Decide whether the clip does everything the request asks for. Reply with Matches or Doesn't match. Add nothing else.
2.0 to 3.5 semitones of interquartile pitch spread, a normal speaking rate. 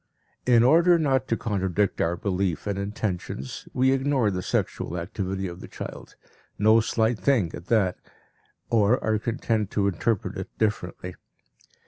Doesn't match